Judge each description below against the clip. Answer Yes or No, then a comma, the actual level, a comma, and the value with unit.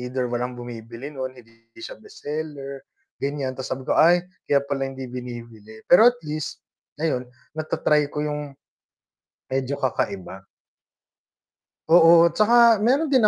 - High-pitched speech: No, medium, 140 Hz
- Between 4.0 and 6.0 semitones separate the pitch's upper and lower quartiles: Yes, average, 4.3 semitones